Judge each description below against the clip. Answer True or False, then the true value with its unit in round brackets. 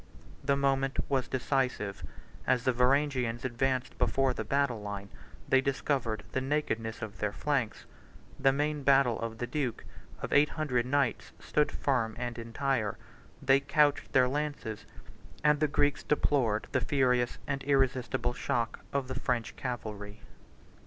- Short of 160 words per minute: True (140 wpm)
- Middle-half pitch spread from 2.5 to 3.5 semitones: True (3.0 semitones)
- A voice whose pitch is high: False (130 Hz)